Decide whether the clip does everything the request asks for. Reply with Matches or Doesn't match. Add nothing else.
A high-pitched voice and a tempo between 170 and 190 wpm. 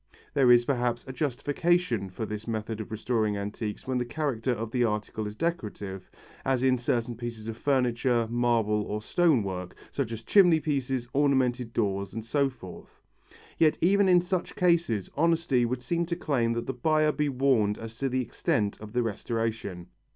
Doesn't match